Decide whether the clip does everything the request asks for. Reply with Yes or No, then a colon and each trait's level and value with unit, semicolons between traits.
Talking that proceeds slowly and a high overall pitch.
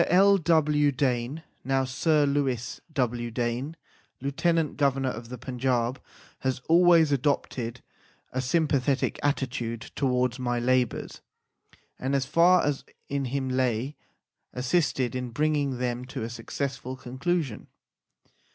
No: slow, 125 wpm; low, 130 Hz